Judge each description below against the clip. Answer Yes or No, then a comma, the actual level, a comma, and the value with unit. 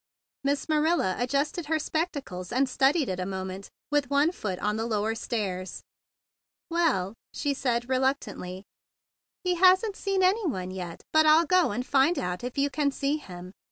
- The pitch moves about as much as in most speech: No, wide, 8.2 semitones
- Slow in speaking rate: No, average, 170 wpm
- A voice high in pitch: Yes, very high, 270 Hz